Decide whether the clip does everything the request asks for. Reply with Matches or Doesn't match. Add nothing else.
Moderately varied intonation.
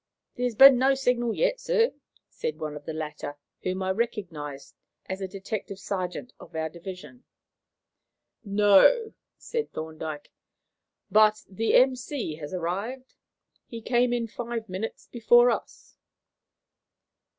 Doesn't match